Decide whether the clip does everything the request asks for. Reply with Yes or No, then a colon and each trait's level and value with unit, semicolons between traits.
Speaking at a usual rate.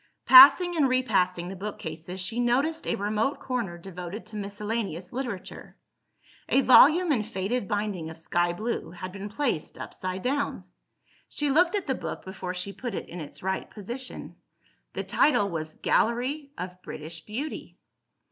Yes: average, 155 wpm